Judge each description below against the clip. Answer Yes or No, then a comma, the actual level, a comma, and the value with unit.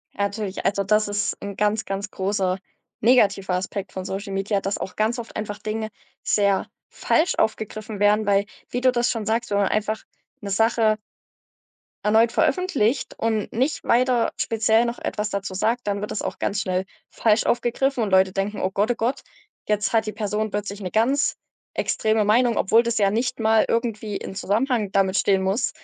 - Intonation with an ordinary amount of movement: No, narrow, 2.3 semitones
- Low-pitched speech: No, high, 215 Hz